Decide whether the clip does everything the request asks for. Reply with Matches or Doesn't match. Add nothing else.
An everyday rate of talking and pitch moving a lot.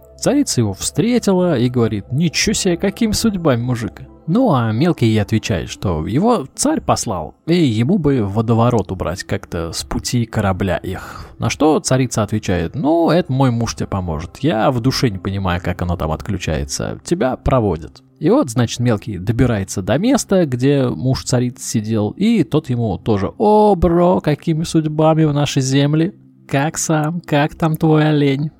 Doesn't match